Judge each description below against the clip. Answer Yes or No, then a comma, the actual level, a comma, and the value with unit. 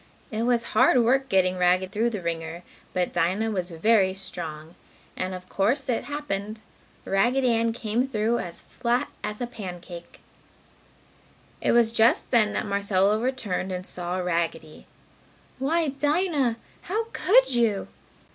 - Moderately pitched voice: No, high, 215 Hz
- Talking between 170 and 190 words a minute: No, average, 140 wpm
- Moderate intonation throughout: Yes, average, 4.9 semitones